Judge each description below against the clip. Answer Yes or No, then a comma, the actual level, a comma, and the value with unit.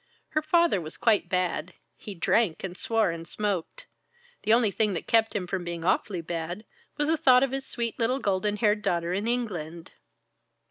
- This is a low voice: No, high, 210 Hz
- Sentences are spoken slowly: No, average, 185 wpm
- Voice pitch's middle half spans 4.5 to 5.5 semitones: Yes, average, 5.1 semitones